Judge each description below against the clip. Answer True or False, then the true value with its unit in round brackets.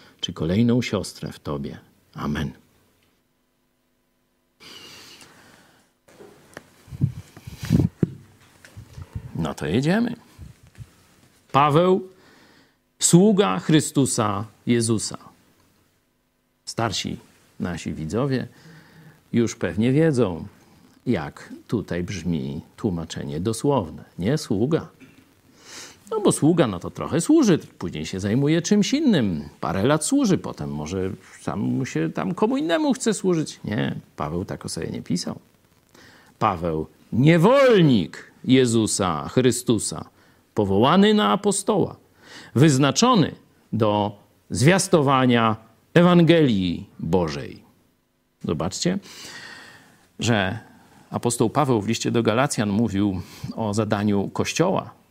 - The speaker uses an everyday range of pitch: False (8.4 semitones)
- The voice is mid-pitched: False (120 Hz)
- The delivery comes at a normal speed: False (90 wpm)